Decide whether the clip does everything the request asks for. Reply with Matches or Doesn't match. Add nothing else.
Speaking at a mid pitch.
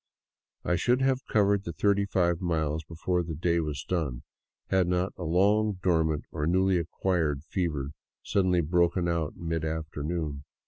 Doesn't match